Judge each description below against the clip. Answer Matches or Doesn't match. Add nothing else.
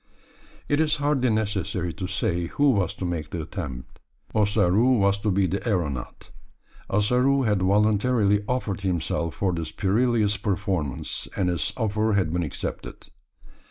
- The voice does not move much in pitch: Doesn't match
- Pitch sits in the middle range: Doesn't match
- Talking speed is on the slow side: Doesn't match